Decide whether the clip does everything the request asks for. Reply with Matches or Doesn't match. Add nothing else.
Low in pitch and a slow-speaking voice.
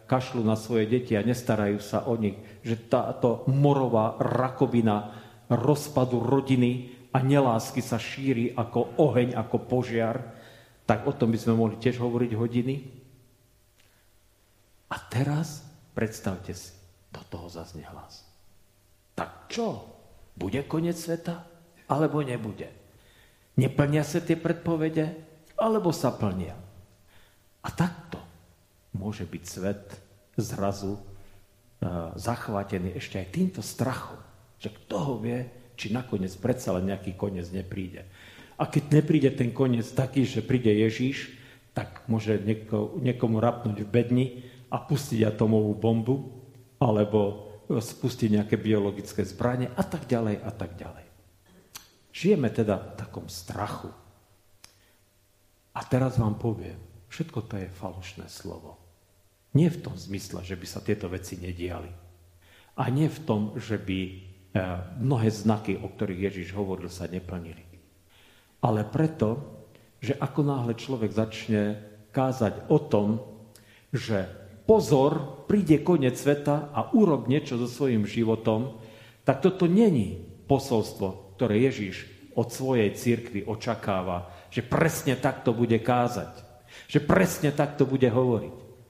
Doesn't match